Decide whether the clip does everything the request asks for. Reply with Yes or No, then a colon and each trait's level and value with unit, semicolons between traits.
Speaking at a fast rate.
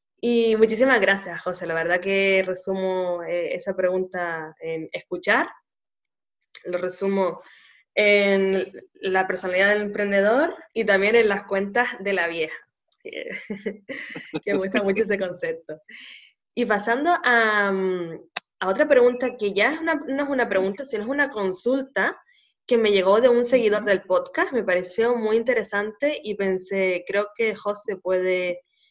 No: average, 145 wpm